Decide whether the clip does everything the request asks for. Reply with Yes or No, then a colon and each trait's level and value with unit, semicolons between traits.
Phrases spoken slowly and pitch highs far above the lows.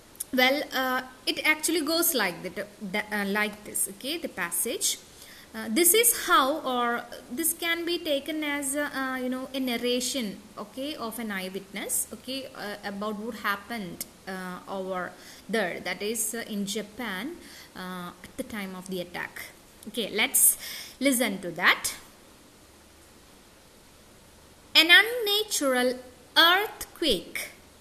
Yes: slow, 130 wpm; wide, 5.7 semitones